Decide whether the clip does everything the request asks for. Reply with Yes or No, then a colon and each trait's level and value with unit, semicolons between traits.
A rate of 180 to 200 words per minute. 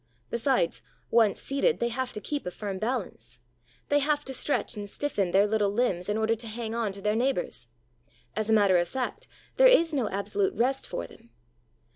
Yes: average, 195 wpm